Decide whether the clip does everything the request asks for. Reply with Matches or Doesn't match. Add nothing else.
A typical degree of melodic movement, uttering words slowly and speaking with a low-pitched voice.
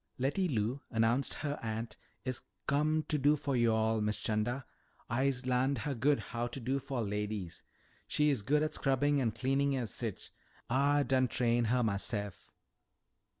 Doesn't match